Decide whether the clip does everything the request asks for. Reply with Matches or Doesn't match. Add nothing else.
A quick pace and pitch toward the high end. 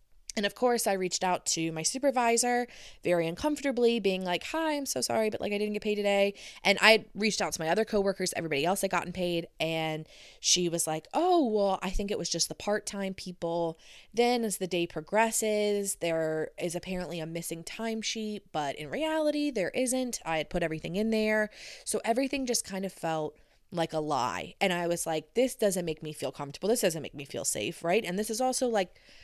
Matches